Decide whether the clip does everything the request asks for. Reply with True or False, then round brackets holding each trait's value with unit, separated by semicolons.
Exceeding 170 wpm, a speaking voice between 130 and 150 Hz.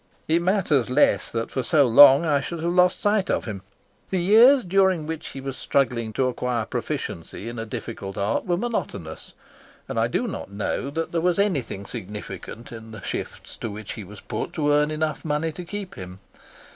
True (195 wpm; 140 Hz)